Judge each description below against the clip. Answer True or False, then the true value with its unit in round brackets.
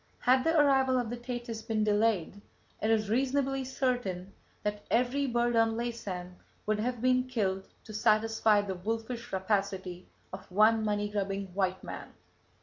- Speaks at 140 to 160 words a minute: True (150 wpm)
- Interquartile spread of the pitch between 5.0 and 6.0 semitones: False (3.6 semitones)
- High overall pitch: True (220 Hz)